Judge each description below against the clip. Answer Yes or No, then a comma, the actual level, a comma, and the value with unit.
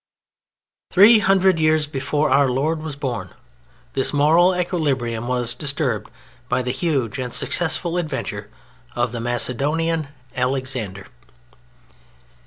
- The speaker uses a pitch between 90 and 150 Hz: Yes, medium, 140 Hz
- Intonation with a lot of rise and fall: No, average, 4.6 semitones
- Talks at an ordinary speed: No, slow, 110 wpm